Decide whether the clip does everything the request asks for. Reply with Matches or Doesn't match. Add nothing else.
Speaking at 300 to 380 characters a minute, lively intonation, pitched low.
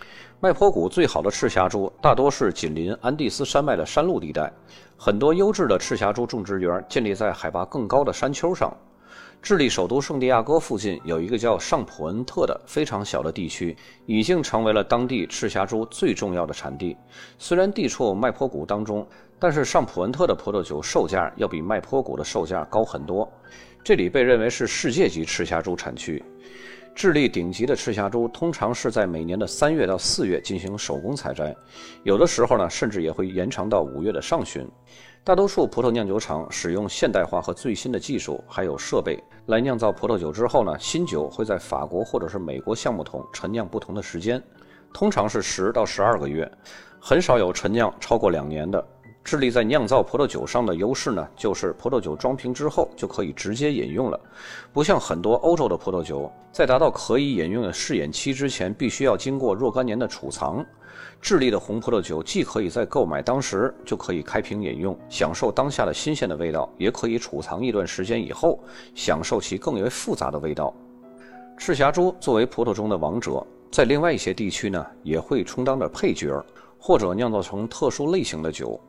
Matches